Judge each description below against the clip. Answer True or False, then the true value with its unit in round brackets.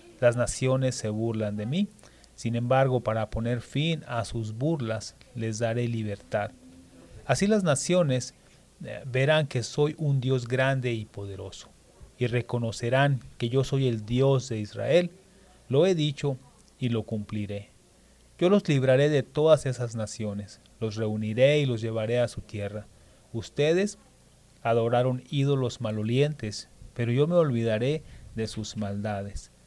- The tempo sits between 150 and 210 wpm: False (140 wpm)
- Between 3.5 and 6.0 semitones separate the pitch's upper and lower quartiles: True (3.9 semitones)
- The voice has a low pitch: True (120 Hz)